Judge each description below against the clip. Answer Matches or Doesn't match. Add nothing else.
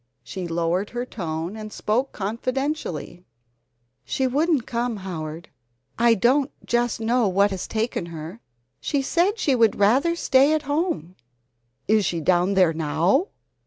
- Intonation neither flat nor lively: Doesn't match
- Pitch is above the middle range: Matches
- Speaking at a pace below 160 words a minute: Matches